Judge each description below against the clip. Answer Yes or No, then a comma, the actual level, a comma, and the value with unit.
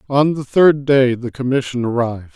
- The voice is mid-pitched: No, low, 130 Hz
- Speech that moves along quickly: No, average, 180 wpm